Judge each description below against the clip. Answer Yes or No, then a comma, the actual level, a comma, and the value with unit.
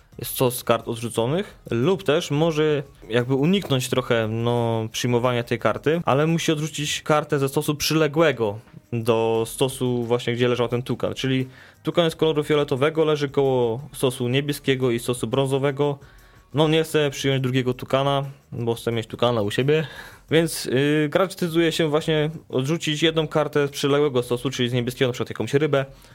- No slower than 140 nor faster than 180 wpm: Yes, fast, 160 wpm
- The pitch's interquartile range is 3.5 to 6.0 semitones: Yes, average, 3.8 semitones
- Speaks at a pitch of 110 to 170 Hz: Yes, low, 135 Hz